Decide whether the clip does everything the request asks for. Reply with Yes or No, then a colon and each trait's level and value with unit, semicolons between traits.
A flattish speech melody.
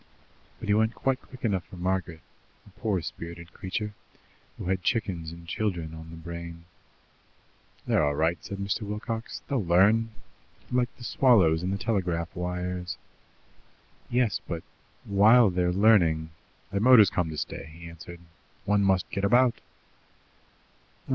No: average, 4.1 semitones